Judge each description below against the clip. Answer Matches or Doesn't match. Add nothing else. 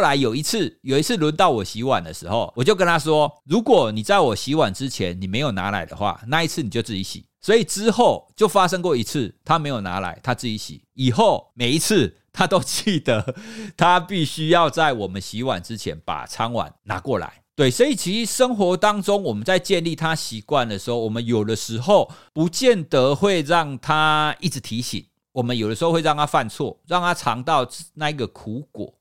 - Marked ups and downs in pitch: Matches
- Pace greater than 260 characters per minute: Matches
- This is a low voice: Doesn't match